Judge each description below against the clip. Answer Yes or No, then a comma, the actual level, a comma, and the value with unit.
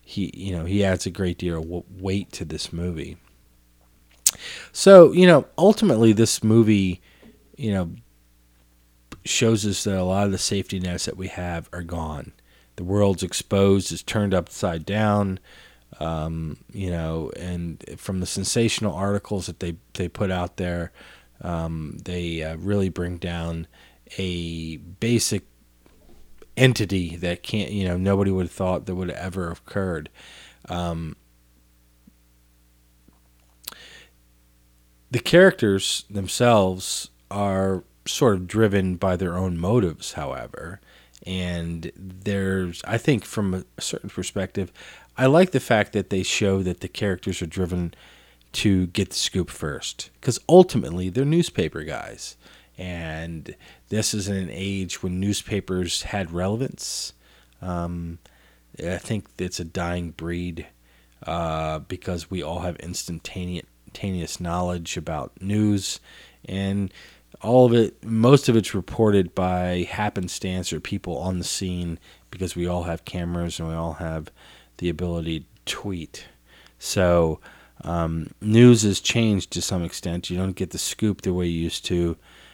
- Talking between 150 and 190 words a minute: No, average, 140 wpm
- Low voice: Yes, very low, 90 Hz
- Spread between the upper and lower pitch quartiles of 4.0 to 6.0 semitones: No, average, 3.1 semitones